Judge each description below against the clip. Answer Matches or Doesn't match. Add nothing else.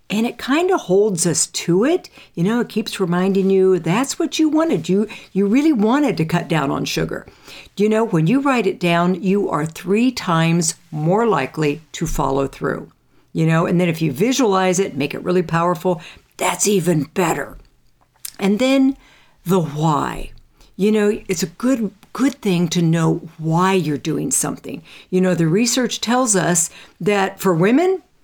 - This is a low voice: Doesn't match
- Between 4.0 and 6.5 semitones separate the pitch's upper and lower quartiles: Matches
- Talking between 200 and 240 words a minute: Doesn't match